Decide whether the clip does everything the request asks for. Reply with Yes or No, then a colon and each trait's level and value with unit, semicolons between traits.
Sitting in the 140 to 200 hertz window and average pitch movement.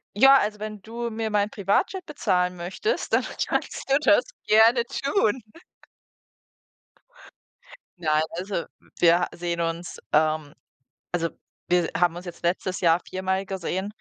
Yes: high, 190 Hz; average, 4.1 semitones